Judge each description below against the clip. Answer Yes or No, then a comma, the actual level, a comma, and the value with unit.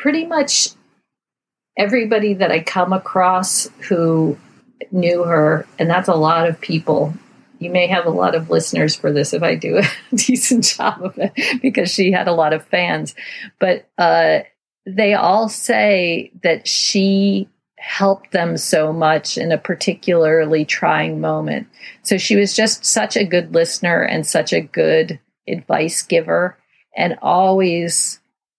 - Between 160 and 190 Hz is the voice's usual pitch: Yes, medium, 185 Hz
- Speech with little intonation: No, average, 4.1 semitones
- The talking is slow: No, average, 150 wpm